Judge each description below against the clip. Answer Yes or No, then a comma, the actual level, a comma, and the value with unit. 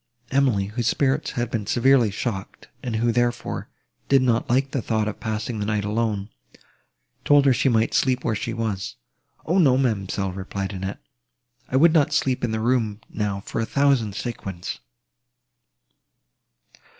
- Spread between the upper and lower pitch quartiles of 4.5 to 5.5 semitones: No, average, 3.7 semitones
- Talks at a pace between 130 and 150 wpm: No, average, 160 wpm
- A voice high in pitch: No, low, 115 Hz